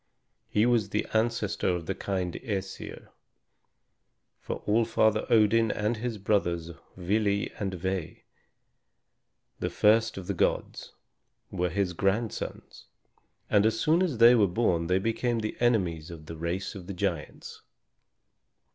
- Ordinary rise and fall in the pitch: Yes, average, 3.8 semitones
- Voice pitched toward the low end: Yes, low, 100 Hz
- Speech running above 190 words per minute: No, slow, 135 wpm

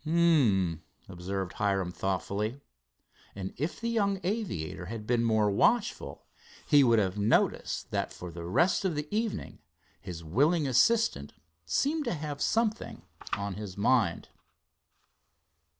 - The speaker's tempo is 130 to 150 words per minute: Yes, slow, 135 wpm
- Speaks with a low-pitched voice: Yes, low, 115 Hz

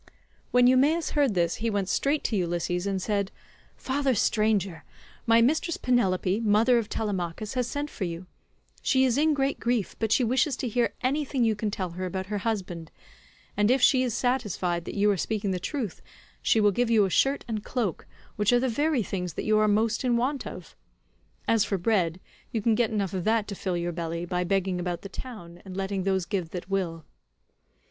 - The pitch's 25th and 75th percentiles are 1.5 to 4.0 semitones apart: No, average, 4.8 semitones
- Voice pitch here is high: Yes, high, 210 Hz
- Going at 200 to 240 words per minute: Yes, fast, 205 wpm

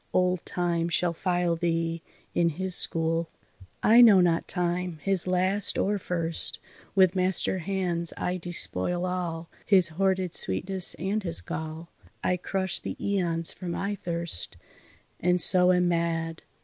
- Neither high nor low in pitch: Yes, medium, 180 Hz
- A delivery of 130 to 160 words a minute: Yes, average, 140 wpm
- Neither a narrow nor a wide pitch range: No, narrow, 1.8 semitones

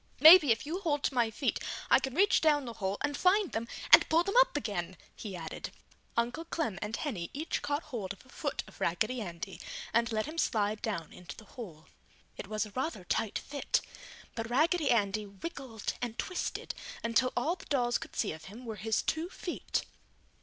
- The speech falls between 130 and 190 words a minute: No, average, 200 wpm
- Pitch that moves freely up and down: Yes, wide, 6.1 semitones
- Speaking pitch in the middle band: No, high, 235 Hz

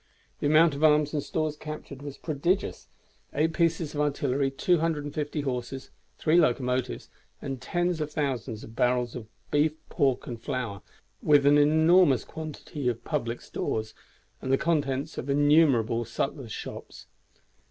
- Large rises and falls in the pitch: No, average, 3.4 semitones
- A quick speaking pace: No, average, 140 wpm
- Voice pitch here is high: No, medium, 145 Hz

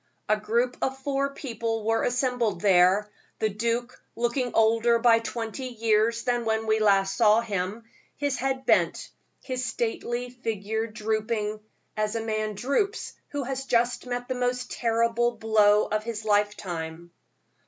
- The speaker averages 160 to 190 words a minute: No, average, 145 wpm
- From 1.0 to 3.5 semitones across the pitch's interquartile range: Yes, narrow, 2.4 semitones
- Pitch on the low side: No, high, 230 Hz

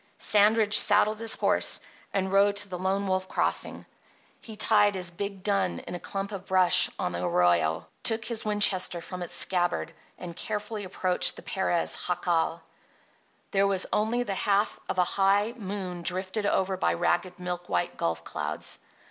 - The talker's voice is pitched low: No, high, 190 Hz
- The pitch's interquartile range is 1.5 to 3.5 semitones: Yes, narrow, 2.6 semitones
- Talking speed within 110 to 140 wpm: No, average, 165 wpm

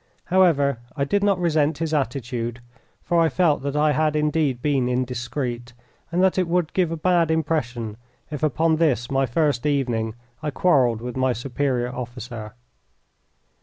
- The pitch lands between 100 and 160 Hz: Yes, medium, 140 Hz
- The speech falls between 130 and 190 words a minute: Yes, average, 160 wpm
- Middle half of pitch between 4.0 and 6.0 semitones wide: Yes, average, 4.7 semitones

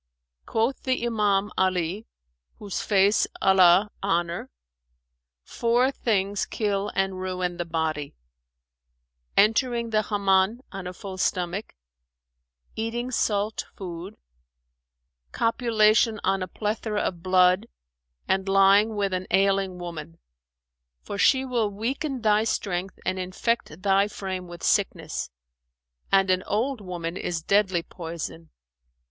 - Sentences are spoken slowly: Yes, slow, 115 wpm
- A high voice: Yes, high, 195 Hz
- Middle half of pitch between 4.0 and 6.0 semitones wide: No, average, 3.0 semitones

